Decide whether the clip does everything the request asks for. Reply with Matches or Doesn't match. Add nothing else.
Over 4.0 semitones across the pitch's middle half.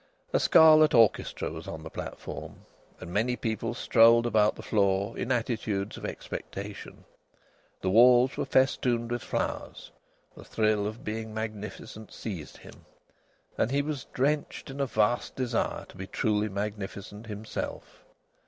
Doesn't match